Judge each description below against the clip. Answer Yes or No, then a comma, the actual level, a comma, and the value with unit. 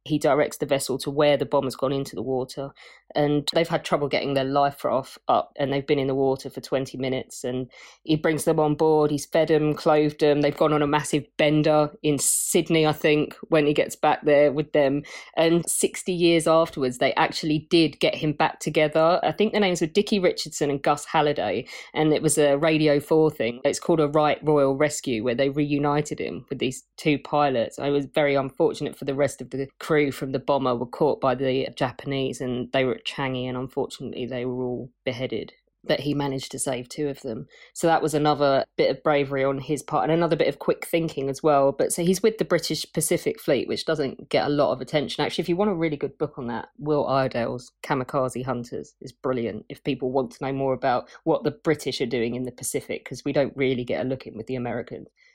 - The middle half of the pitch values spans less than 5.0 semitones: Yes, narrow, 2.6 semitones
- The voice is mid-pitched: Yes, medium, 145 Hz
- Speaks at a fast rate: Yes, fast, 230 wpm